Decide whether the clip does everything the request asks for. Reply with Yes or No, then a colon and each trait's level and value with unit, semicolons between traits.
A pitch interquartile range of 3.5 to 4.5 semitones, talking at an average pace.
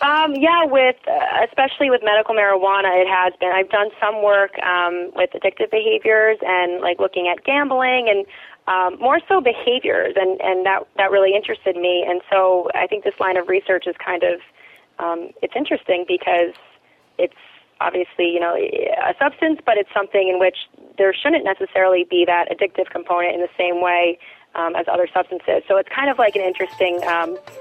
Yes: average, 4.2 semitones; average, 185 wpm